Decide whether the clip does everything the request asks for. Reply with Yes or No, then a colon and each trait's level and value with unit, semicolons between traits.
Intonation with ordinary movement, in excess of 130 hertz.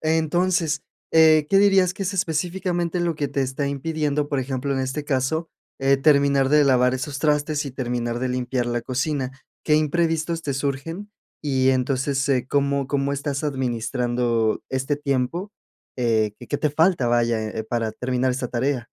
Yes: average, 3.4 semitones; medium, 140 Hz